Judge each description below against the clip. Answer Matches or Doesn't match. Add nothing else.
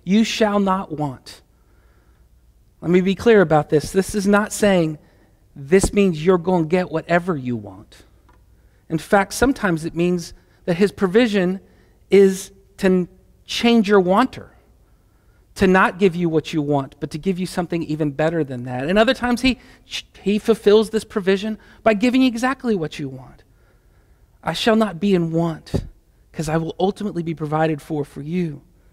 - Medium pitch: Matches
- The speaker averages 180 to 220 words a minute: Doesn't match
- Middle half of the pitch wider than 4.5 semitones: Matches